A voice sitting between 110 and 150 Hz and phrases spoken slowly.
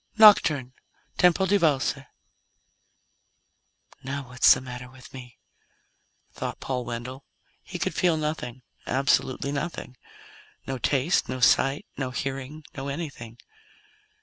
Yes: low, 135 Hz; slow, 120 wpm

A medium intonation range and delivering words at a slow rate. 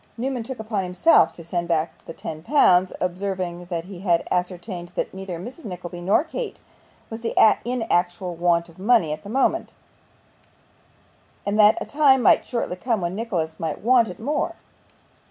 No: average, 4.8 semitones; average, 170 wpm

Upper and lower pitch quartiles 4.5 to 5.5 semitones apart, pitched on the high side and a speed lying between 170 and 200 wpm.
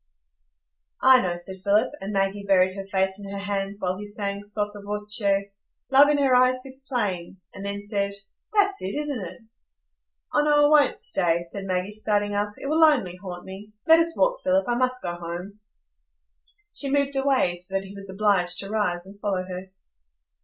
Yes: average, 5.0 semitones; high, 205 Hz; average, 190 wpm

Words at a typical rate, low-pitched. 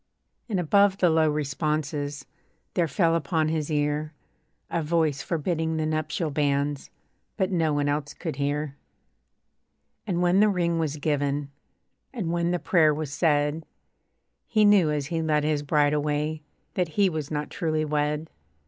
No: average, 155 wpm; medium, 155 Hz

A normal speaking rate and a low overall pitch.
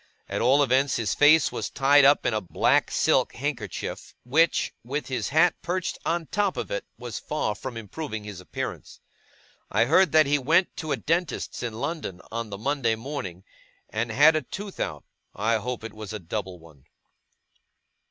Yes: average, 180 wpm; low, 130 Hz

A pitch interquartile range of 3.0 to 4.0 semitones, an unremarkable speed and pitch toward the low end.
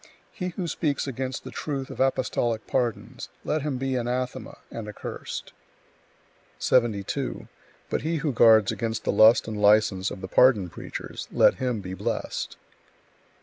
Yes: average, 3.7 semitones; average, 150 wpm; low, 120 Hz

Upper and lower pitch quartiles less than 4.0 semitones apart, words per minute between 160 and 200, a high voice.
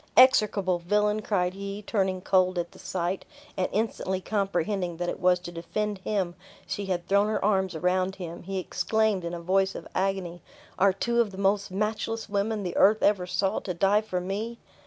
Yes: narrow, 2.4 semitones; average, 190 wpm; high, 195 Hz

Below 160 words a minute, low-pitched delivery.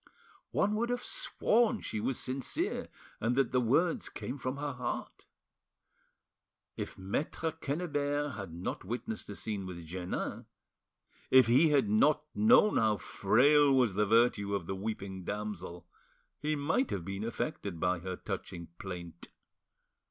Yes: average, 145 wpm; low, 115 Hz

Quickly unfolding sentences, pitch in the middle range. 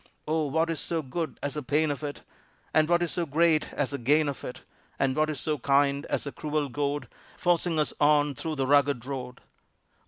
Yes: fast, 215 wpm; medium, 145 Hz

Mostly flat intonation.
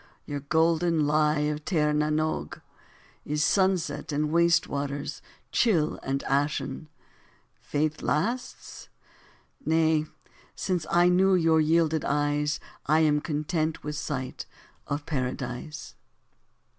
Yes: narrow, 1.8 semitones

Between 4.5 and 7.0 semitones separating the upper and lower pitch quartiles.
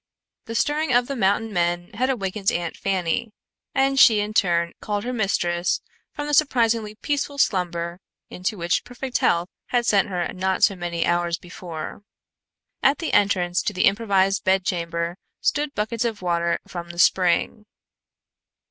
Yes: average, 4.9 semitones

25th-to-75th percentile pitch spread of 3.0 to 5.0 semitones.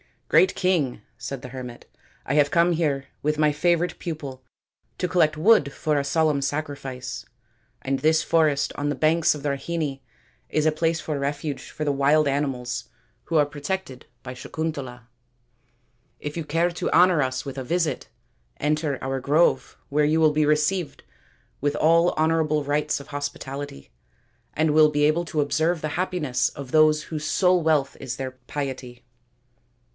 No: narrow, 2.5 semitones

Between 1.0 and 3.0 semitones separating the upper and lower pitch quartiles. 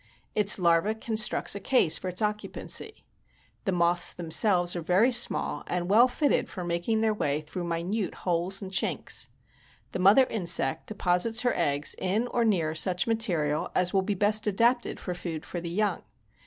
No: average, 3.9 semitones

